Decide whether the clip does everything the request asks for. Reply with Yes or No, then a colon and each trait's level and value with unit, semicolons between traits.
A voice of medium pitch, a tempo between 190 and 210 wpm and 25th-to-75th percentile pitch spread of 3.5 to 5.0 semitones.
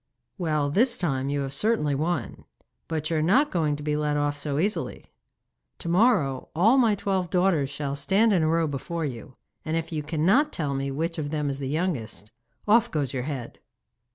Yes: medium, 155 Hz; average, 200 wpm; average, 4.3 semitones